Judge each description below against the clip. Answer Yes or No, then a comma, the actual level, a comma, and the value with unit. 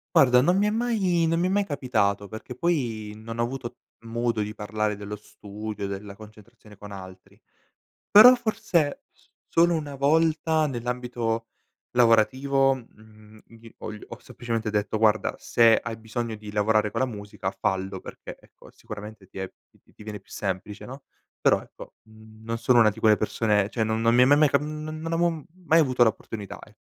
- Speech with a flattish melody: No, average, 4.9 semitones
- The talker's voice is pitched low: Yes, low, 115 Hz